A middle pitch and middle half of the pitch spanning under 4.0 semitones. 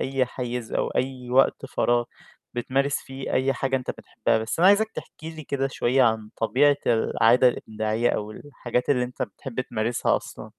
No: low, 125 Hz; narrow, 2.4 semitones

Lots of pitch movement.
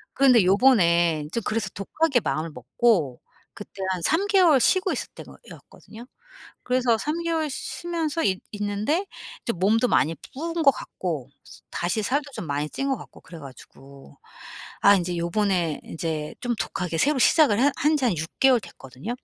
Yes: wide, 8.4 semitones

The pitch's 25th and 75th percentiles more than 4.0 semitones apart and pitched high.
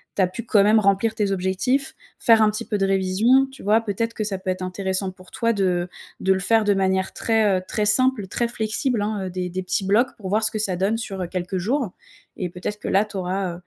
No: average, 2.9 semitones; high, 200 Hz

